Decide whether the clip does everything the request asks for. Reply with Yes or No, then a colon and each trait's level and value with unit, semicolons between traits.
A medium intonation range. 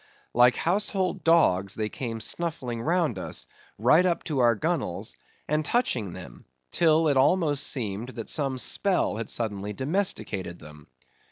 No: wide, 7.2 semitones